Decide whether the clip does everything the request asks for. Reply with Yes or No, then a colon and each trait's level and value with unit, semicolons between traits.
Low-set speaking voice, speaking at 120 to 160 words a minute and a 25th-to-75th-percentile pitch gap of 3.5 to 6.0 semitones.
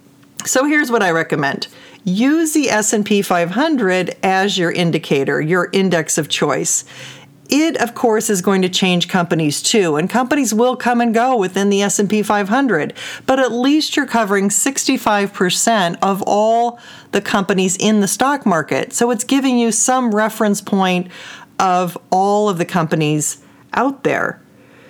No: high, 210 Hz; average, 150 wpm; average, 4.8 semitones